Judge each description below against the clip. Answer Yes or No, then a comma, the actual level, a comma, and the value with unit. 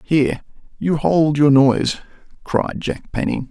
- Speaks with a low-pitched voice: No, medium, 145 Hz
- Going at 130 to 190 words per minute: Yes, slow, 135 wpm